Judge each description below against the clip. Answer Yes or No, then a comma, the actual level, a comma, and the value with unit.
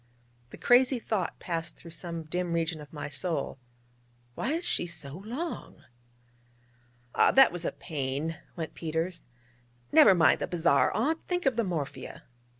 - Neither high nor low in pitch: Yes, medium, 170 Hz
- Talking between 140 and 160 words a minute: Yes, average, 150 wpm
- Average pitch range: No, wide, 6.4 semitones